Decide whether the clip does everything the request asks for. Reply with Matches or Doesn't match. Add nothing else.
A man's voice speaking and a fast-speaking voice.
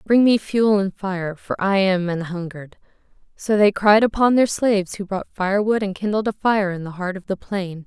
Doesn't match